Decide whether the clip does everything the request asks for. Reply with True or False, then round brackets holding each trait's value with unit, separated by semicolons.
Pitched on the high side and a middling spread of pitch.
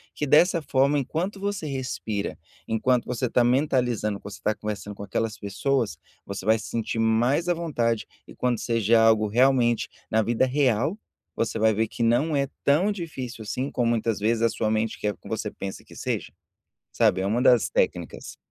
False (120 Hz; 3.8 semitones)